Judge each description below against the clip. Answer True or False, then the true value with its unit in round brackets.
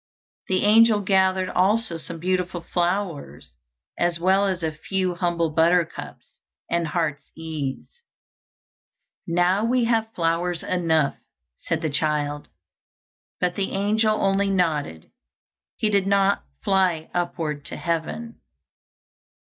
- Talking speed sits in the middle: False (115 wpm)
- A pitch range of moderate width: True (3.2 semitones)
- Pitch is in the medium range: True (180 Hz)